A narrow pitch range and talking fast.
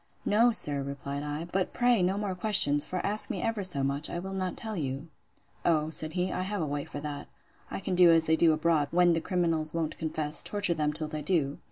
No: average, 3.8 semitones; fast, 235 wpm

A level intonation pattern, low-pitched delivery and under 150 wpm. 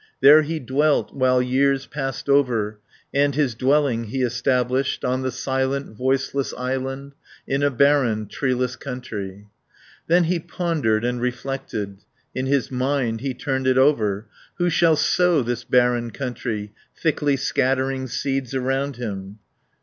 Yes: narrow, 2.3 semitones; low, 130 Hz; average, 140 wpm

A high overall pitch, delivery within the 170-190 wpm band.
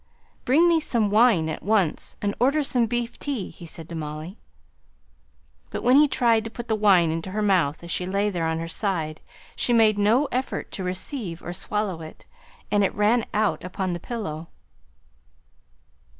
Yes: high, 205 Hz; average, 180 wpm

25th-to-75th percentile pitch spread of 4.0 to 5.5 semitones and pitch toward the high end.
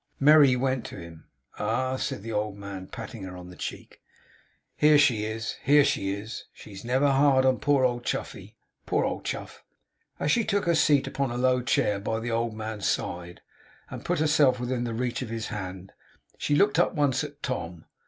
No: average, 4.9 semitones; low, 125 Hz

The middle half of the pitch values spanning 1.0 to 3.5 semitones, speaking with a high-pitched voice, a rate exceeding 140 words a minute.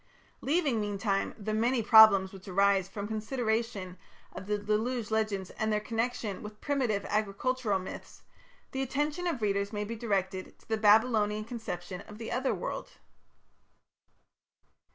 No: average, 2.7 semitones; high, 215 Hz; slow, 135 wpm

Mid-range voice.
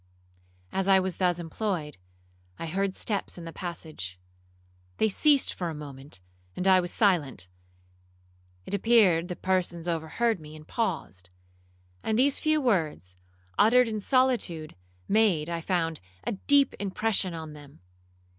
Yes: medium, 180 Hz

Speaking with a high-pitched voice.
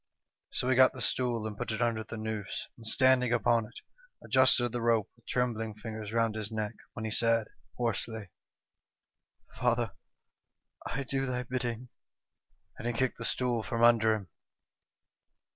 No: low, 115 Hz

